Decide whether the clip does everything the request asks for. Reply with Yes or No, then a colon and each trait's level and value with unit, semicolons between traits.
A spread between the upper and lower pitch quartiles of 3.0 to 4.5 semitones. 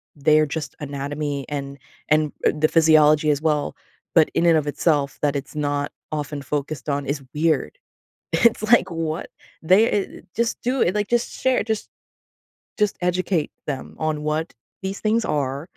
Yes: average, 3.6 semitones